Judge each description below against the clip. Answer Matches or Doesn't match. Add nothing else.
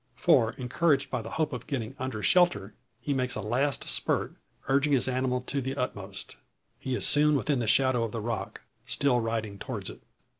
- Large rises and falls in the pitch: Doesn't match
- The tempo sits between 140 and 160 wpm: Doesn't match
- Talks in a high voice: Doesn't match